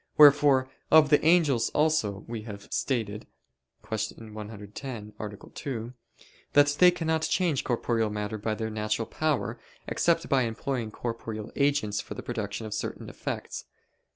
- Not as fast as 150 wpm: Yes, average, 140 wpm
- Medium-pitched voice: No, low, 115 Hz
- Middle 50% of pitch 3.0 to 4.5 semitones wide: No, average, 5.1 semitones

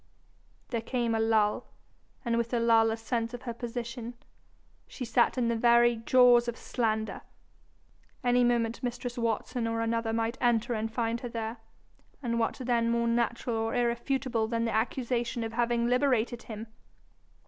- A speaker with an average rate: Yes, average, 160 wpm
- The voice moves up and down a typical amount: No, narrow, 1.1 semitones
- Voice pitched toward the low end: No, high, 235 Hz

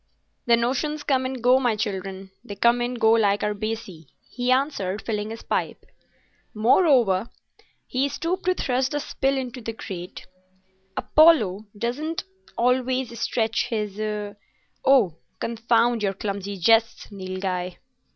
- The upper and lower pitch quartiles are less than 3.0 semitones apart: No, average, 4.1 semitones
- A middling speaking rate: No, slow, 130 wpm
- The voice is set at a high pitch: Yes, high, 225 Hz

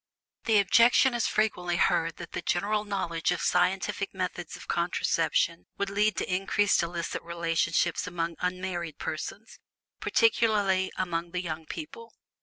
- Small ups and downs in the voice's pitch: No, average, 3.2 semitones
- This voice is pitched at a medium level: Yes, medium, 180 Hz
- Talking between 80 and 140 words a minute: Yes, slow, 135 wpm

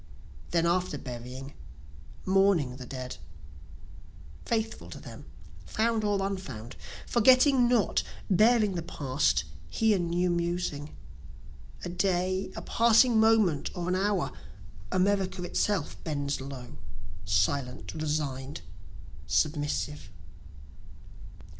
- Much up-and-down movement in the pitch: Yes, wide, 6.3 semitones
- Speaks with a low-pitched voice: No, medium, 175 Hz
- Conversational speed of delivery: No, slow, 95 wpm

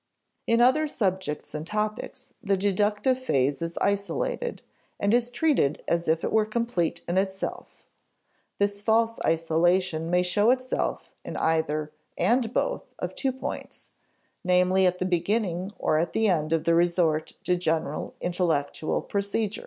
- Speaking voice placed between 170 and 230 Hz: Yes, medium, 185 Hz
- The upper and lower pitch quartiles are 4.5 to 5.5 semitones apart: Yes, average, 4.8 semitones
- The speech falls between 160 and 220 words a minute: No, average, 145 wpm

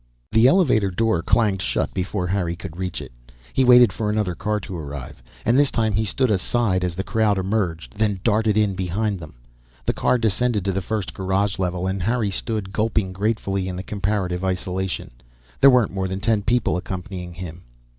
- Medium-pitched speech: No, low, 100 Hz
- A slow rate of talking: No, average, 190 wpm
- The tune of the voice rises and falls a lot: No, average, 3.1 semitones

